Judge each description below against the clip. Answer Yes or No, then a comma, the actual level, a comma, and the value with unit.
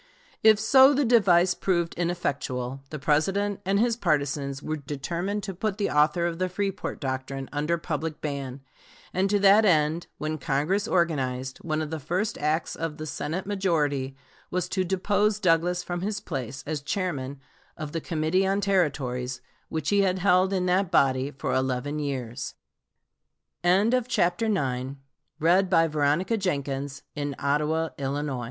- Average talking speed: No, slow, 130 wpm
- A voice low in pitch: No, medium, 170 Hz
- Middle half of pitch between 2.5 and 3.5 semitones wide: No, average, 4.8 semitones